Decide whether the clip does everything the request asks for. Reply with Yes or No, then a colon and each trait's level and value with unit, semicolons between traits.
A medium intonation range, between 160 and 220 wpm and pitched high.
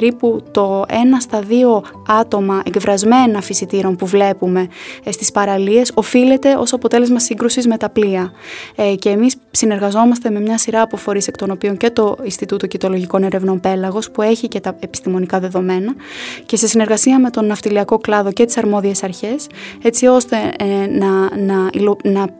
Yes: average, 3.0 semitones; average, 165 wpm; high, 210 Hz